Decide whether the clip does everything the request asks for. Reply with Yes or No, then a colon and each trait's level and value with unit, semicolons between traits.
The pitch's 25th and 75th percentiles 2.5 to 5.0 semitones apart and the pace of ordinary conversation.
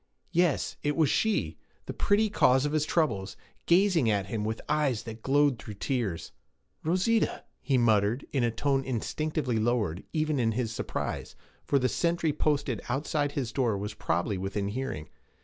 No: wide, 5.6 semitones; average, 165 wpm